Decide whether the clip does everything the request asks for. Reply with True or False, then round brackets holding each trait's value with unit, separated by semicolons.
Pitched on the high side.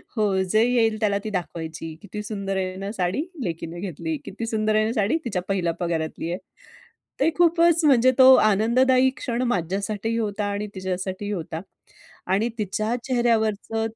True (210 Hz)